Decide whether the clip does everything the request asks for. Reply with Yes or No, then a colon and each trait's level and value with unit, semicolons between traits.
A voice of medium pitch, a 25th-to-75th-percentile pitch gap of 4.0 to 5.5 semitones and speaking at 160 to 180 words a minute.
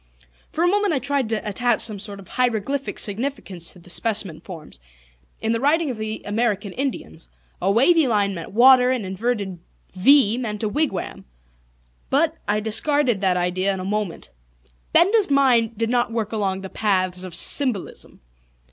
No: high, 220 Hz; average, 5.1 semitones; average, 165 wpm